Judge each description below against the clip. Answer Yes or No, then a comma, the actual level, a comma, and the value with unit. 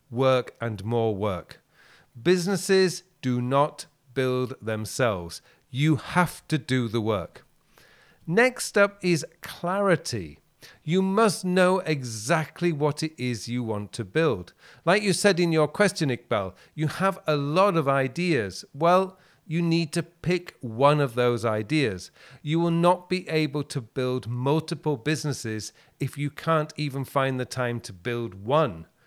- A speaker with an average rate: Yes, average, 145 wpm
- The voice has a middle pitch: Yes, medium, 150 Hz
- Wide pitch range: Yes, wide, 5.9 semitones